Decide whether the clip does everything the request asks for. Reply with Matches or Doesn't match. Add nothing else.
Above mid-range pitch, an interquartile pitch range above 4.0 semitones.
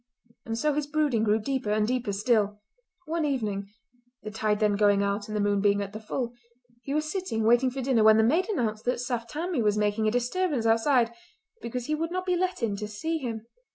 Matches